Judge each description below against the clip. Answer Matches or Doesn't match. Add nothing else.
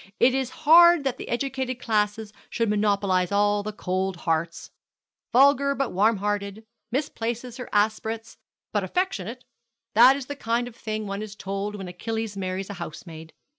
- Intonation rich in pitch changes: Doesn't match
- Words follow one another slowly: Doesn't match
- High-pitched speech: Matches